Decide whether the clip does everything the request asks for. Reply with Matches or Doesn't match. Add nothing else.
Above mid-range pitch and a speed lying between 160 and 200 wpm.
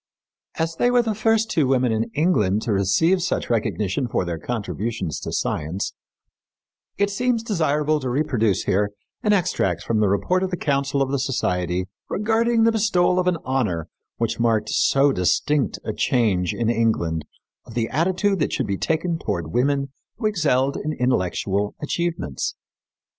Doesn't match